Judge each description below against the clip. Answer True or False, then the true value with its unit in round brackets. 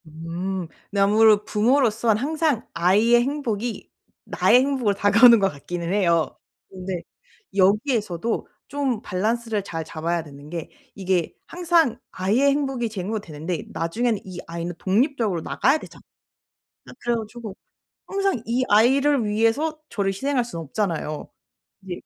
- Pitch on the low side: False (210 Hz)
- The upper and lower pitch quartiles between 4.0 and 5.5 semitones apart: True (5.2 semitones)